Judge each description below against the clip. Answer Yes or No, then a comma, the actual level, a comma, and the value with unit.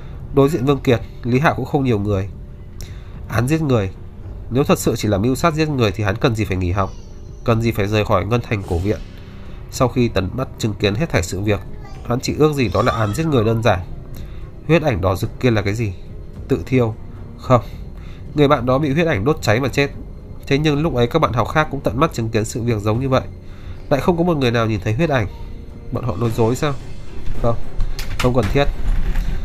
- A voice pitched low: Yes, low, 115 Hz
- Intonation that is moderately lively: Yes, average, 4.9 semitones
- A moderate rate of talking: Yes, average, 240 wpm